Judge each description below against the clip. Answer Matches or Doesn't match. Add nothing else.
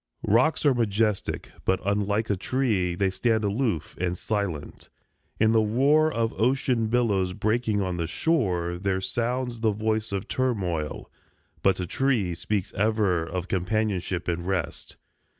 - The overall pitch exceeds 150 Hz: Doesn't match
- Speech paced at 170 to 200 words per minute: Doesn't match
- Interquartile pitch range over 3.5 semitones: Matches